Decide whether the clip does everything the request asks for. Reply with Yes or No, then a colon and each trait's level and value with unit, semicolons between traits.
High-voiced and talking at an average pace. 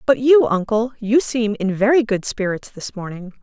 Yes: high, 225 Hz; average, 195 wpm